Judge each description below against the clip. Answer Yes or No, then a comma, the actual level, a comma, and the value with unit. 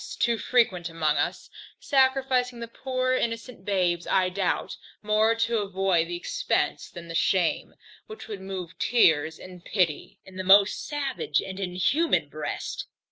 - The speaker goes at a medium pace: Yes, average, 145 wpm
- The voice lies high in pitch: Yes, high, 195 Hz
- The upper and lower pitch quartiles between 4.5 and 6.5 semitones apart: Yes, average, 4.8 semitones